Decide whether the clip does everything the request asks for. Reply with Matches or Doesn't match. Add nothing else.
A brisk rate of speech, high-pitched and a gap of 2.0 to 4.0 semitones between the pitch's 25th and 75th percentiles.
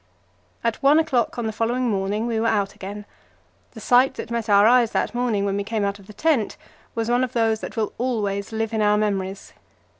Matches